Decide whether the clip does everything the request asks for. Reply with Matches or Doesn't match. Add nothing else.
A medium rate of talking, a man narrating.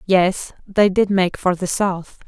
Doesn't match